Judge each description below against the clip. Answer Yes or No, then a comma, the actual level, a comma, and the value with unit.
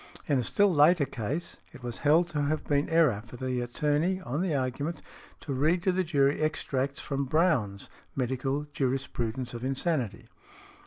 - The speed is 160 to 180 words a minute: Yes, average, 165 wpm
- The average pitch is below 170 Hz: Yes, medium, 140 Hz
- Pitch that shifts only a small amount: No, average, 3.8 semitones